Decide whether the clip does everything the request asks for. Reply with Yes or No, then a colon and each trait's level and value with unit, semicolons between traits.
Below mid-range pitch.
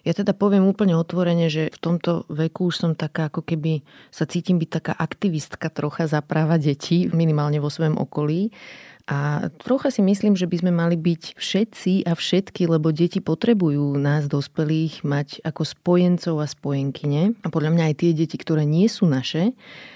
No: medium, 165 Hz